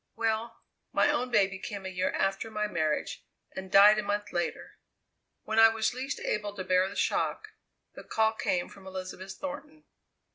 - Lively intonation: No, average, 2.9 semitones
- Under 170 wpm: No, average, 175 wpm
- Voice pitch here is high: Yes, high, 205 Hz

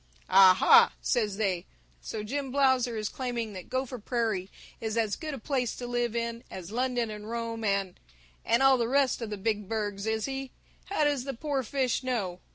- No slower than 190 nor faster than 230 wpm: Yes, average, 195 wpm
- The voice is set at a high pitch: Yes, high, 230 Hz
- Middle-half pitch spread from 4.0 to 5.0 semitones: No, average, 3.6 semitones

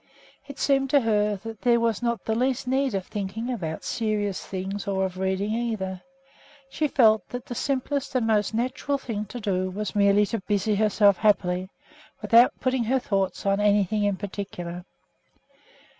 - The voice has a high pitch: Yes, high, 210 Hz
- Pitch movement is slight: No, average, 3.5 semitones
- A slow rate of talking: No, average, 170 wpm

